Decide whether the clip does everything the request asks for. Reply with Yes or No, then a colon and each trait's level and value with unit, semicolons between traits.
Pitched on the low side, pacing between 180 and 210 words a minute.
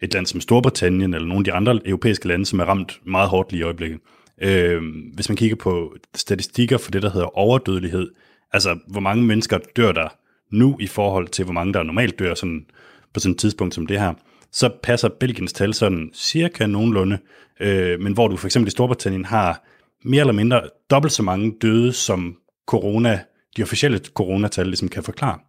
Yes: low, 100 Hz; average, 200 wpm